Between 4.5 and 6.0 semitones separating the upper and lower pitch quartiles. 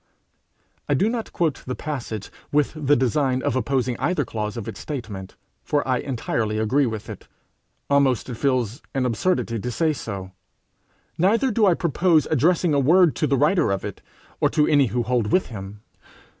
Yes: average, 4.9 semitones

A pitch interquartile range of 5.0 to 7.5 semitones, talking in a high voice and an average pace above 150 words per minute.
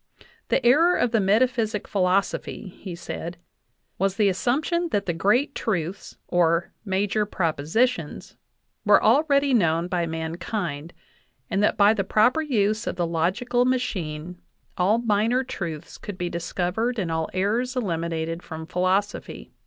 No: wide, 5.5 semitones; high, 195 Hz; average, 140 wpm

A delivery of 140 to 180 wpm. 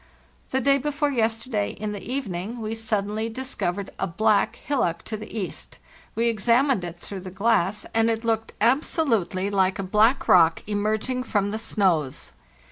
Yes: average, 170 wpm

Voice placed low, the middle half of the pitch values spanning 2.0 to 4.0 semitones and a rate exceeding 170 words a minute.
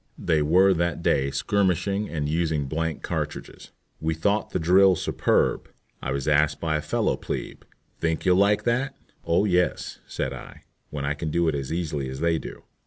Yes: very low, 80 Hz; average, 3.7 semitones; average, 180 wpm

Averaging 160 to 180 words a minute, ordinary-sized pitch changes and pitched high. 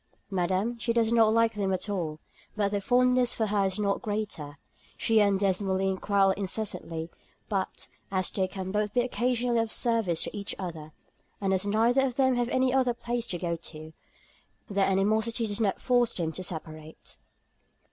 Yes: average, 175 wpm; average, 3.7 semitones; high, 205 Hz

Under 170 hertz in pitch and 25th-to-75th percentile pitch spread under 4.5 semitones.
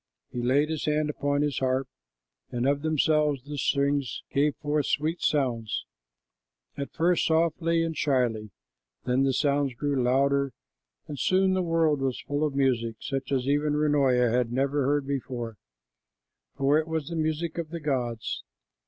Yes: medium, 140 Hz; narrow, 2.6 semitones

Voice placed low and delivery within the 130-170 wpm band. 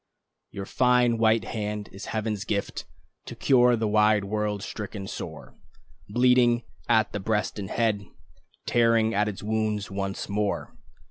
Yes: low, 105 Hz; average, 140 wpm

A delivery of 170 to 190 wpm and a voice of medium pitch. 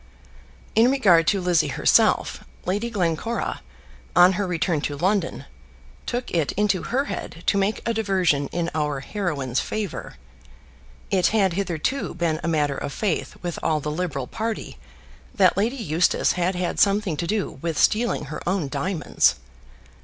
No: average, 155 wpm; medium, 180 Hz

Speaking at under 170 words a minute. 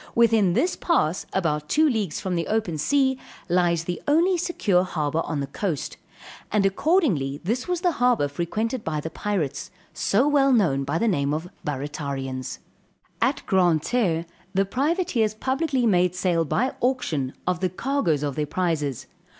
Yes: average, 160 wpm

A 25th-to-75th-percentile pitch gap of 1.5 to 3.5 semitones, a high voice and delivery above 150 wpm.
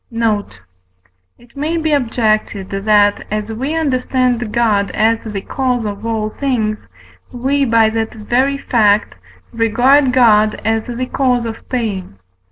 No: average, 3.1 semitones; high, 230 Hz; slow, 135 wpm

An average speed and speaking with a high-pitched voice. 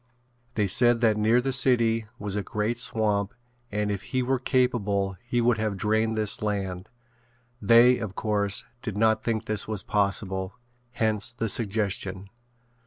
No: average, 155 wpm; low, 110 Hz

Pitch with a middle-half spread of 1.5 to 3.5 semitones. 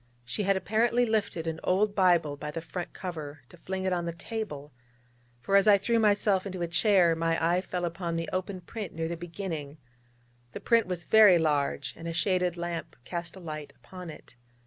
Yes: average, 3.2 semitones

